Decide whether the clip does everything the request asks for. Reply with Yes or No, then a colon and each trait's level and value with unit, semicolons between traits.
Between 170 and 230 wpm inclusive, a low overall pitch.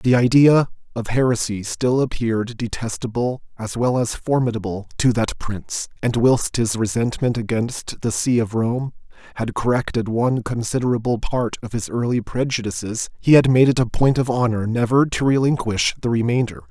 No: average, 160 wpm; low, 120 Hz